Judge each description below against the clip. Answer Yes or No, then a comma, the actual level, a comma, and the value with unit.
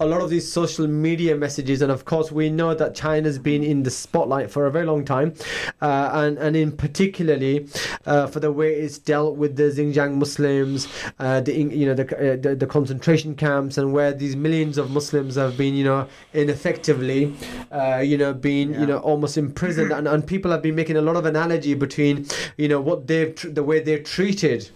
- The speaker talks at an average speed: No, fast, 215 wpm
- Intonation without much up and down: Yes, narrow, 1.7 semitones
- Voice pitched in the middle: Yes, medium, 150 Hz